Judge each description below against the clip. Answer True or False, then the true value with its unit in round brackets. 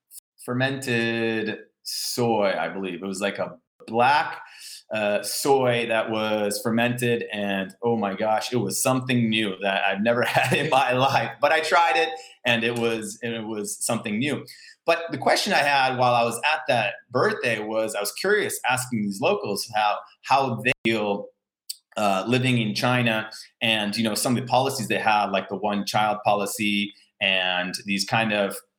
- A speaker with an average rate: True (175 wpm)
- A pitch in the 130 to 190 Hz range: False (110 Hz)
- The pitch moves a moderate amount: True (3.0 semitones)